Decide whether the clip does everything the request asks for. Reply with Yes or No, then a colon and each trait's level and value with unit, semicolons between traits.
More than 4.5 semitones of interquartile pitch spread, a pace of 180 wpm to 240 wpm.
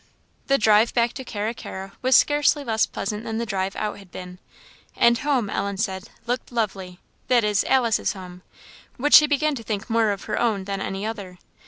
No: average, 3.5 semitones; average, 190 wpm